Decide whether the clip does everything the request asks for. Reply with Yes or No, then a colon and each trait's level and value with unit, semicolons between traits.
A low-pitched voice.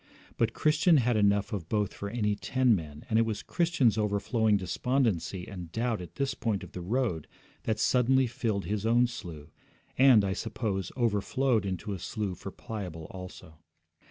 Yes: low, 105 Hz